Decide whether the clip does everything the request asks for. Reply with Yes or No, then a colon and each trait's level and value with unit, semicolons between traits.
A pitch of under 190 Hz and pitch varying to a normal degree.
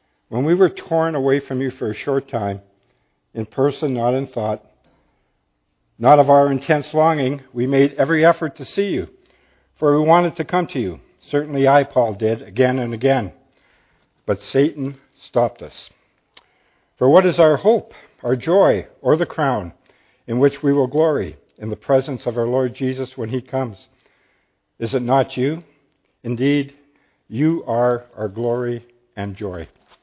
Yes: low, 135 Hz; average, 3.2 semitones